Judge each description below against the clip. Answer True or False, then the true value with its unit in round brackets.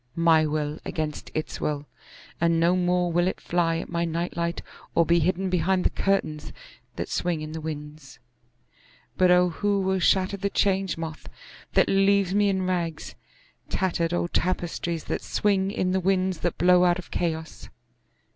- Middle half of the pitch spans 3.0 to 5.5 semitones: False (2.6 semitones)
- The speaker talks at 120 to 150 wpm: False (165 wpm)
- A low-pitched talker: False (175 Hz)